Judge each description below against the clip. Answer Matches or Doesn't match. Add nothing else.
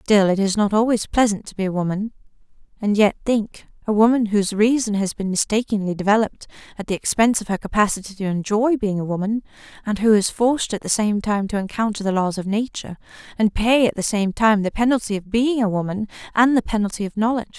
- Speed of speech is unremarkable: Doesn't match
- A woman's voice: Matches